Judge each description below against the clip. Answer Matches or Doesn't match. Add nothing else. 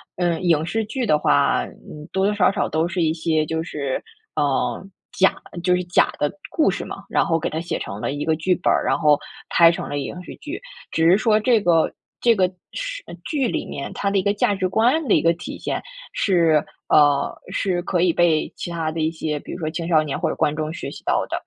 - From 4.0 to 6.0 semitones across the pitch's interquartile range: Doesn't match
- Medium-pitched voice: Matches